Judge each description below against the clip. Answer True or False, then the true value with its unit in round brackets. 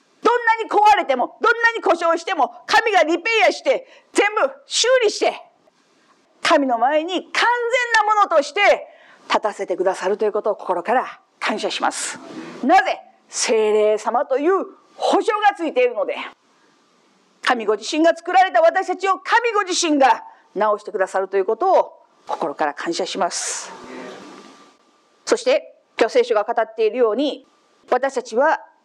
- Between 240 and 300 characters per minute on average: True (295 characters per minute)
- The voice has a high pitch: True (335 Hz)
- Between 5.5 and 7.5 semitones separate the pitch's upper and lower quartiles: False (8.5 semitones)